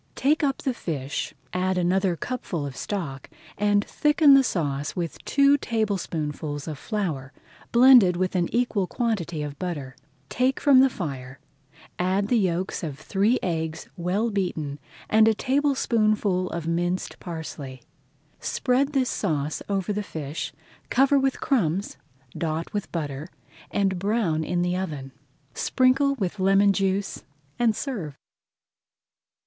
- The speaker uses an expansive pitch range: Yes, wide, 6.3 semitones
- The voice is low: No, high, 190 Hz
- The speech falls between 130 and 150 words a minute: Yes, slow, 135 wpm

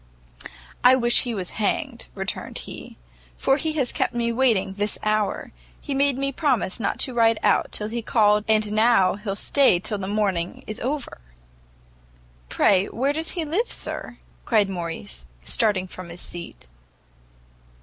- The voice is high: Yes, high, 215 Hz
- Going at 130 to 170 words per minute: Yes, average, 160 wpm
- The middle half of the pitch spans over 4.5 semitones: Yes, average, 4.9 semitones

